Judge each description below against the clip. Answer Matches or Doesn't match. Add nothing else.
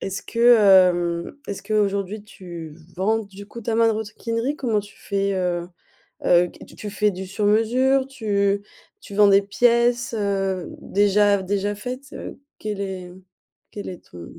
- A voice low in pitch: Doesn't match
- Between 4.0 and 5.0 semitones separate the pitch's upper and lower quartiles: Doesn't match